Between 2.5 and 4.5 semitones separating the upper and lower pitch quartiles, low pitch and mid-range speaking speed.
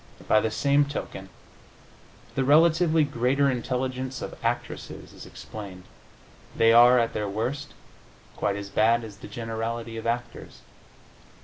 No: average, 3.5 semitones; low, 120 Hz; slow, 130 wpm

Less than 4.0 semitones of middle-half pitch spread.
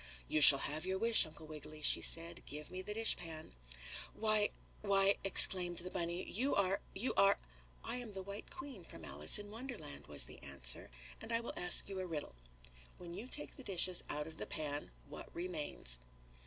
No: average, 5.0 semitones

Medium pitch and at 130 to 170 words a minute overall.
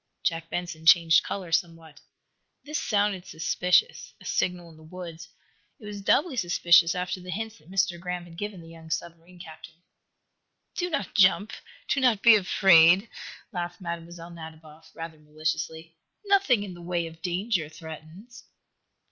Yes: medium, 175 Hz; average, 150 wpm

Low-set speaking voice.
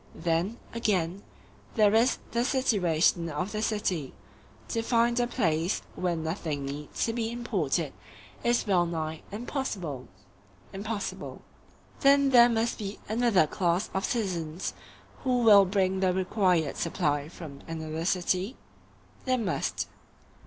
No: high, 190 Hz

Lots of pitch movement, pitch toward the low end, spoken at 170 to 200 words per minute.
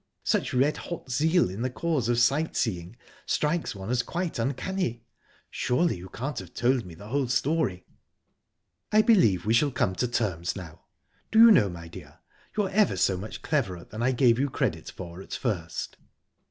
Yes: wide, 7.8 semitones; low, 120 Hz; average, 180 wpm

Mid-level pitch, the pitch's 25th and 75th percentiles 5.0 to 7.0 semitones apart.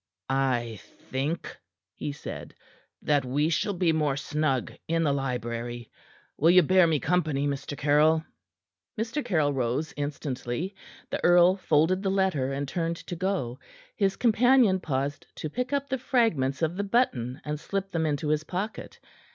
Yes: medium, 155 Hz; wide, 5.4 semitones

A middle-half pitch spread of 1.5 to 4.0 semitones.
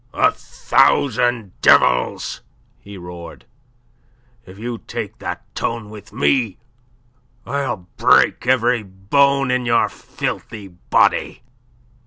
No: average, 4.6 semitones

